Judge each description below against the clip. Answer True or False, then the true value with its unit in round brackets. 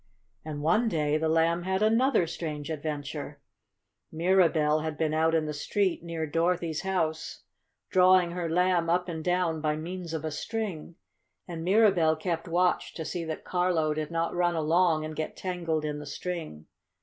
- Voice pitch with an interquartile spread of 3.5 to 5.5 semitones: False (2.4 semitones)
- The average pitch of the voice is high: False (165 Hz)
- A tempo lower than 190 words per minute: True (170 wpm)